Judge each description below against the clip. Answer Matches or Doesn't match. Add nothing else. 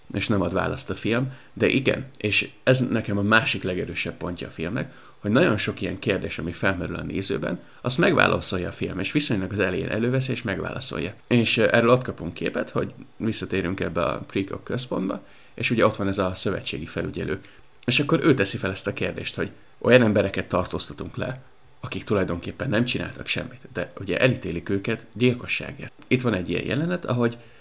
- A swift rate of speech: Matches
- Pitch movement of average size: Matches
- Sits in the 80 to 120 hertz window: Matches